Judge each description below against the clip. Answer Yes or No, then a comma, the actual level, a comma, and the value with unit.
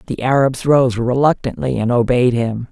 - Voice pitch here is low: Yes, low, 125 Hz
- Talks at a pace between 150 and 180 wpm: Yes, average, 155 wpm